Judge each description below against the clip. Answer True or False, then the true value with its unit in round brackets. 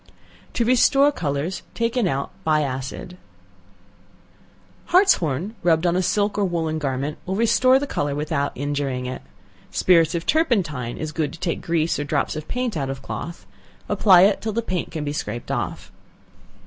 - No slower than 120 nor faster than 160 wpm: False (170 wpm)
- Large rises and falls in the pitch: True (6.1 semitones)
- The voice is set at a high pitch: False (165 Hz)